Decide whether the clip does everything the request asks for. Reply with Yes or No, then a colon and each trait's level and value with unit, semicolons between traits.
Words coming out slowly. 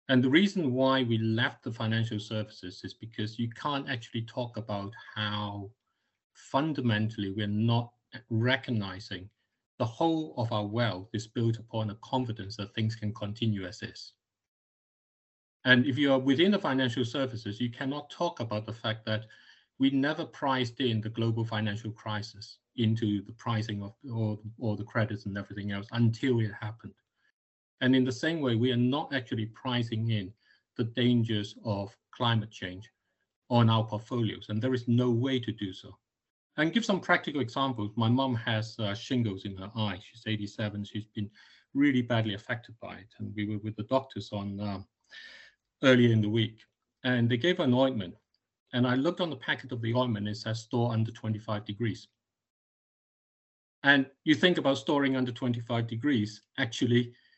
No: average, 170 wpm